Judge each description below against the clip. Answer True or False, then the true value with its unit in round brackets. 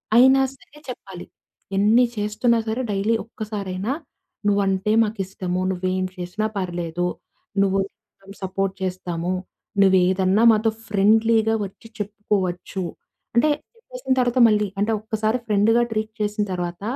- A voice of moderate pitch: False (205 Hz)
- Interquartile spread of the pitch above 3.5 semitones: False (3.0 semitones)